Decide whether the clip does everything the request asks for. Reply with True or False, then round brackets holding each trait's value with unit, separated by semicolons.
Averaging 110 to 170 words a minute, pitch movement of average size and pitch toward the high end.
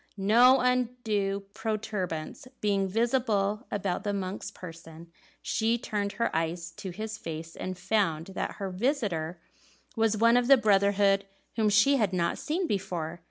True (145 wpm; 3.6 semitones; 200 Hz)